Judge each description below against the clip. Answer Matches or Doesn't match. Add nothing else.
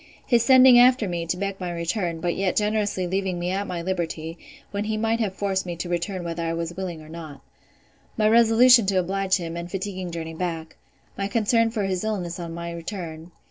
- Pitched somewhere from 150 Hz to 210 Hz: Matches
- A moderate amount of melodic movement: Matches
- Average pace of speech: Doesn't match